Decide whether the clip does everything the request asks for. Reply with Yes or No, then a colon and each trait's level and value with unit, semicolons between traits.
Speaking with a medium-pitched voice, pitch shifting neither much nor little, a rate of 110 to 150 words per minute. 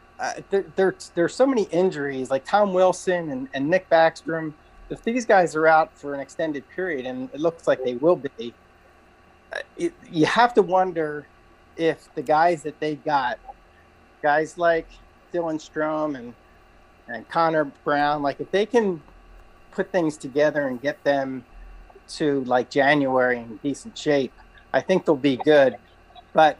No: medium, 155 Hz; average, 4.4 semitones; average, 165 wpm